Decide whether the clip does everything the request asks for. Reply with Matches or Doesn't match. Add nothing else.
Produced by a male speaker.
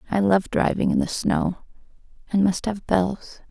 Doesn't match